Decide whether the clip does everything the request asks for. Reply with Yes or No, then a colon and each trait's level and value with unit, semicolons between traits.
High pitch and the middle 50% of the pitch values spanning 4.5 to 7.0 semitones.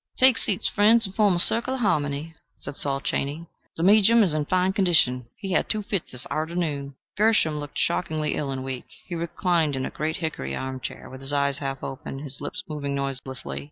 No: medium, 155 Hz; average, 5.3 semitones